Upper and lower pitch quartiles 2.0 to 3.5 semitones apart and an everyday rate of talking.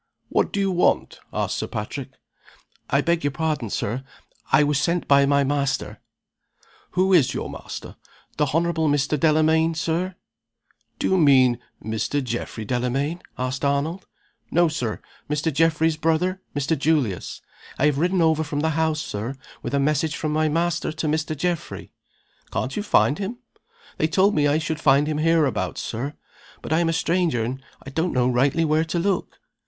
Yes: average, 2.8 semitones; average, 170 wpm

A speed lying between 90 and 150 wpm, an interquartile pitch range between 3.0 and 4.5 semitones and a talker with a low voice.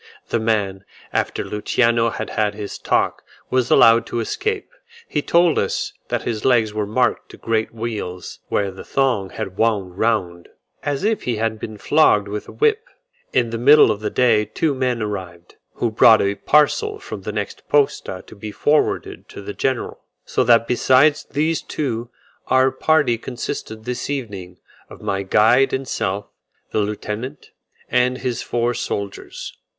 No: average, 165 wpm; average, 4.0 semitones; low, 115 Hz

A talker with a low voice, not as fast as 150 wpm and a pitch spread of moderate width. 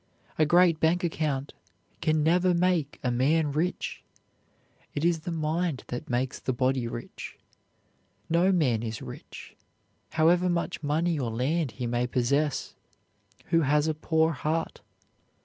No: medium, 155 Hz; average, 140 wpm; average, 4.2 semitones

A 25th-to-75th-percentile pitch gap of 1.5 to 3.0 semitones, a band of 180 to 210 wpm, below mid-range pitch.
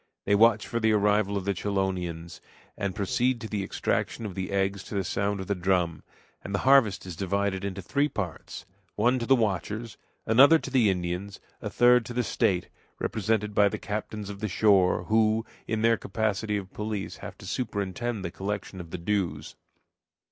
Yes: narrow, 2.6 semitones; average, 190 wpm; low, 100 Hz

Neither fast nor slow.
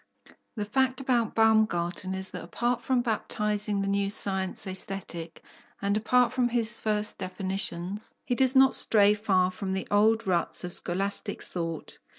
Yes: average, 155 wpm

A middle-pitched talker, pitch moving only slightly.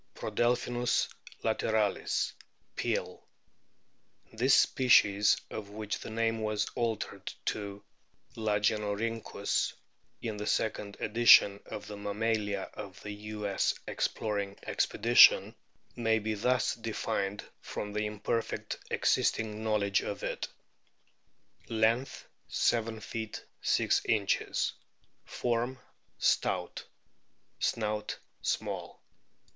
No: low, 110 Hz; narrow, 1.7 semitones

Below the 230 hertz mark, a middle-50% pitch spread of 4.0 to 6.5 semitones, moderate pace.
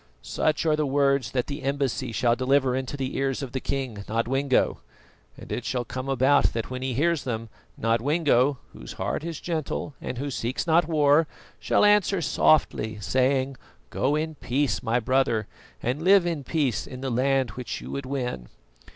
No: low, 135 Hz; average, 2.8 semitones; average, 175 wpm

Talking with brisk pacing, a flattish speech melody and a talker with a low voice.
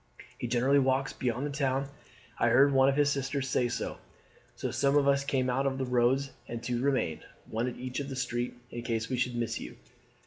Yes: fast, 235 wpm; narrow, 2.2 semitones; low, 130 Hz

